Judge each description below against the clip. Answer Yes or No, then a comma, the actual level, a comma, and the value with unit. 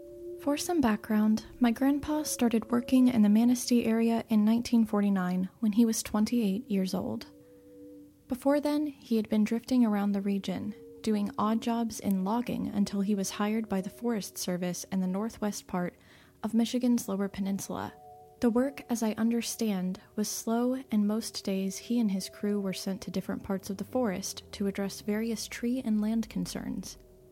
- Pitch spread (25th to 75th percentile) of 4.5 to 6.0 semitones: No, average, 3.3 semitones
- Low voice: No, high, 215 Hz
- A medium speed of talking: Yes, average, 170 wpm